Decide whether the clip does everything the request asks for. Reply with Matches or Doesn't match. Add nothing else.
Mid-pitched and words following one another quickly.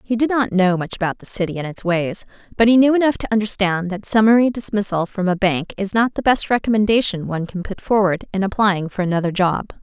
Doesn't match